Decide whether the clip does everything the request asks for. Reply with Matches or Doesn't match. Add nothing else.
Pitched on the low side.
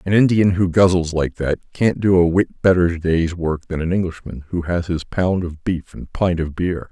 Matches